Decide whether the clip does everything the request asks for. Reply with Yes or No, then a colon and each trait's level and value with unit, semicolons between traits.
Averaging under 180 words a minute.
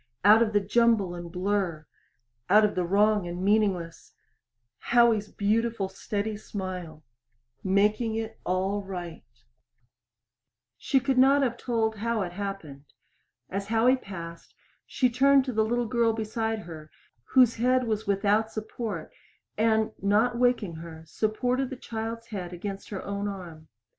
Yes: average, 140 wpm